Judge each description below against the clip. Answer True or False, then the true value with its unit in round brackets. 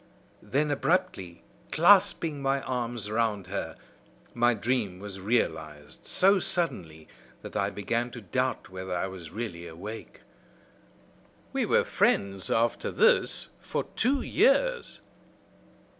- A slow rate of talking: True (115 wpm)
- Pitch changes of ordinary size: False (7.2 semitones)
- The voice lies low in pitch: True (115 Hz)